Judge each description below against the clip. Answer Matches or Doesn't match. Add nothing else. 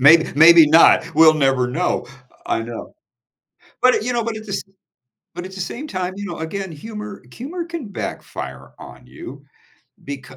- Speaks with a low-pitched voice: Doesn't match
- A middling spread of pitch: Doesn't match